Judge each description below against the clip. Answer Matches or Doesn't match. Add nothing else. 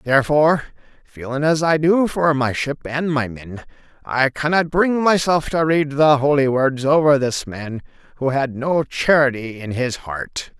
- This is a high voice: Doesn't match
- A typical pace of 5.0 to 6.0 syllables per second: Doesn't match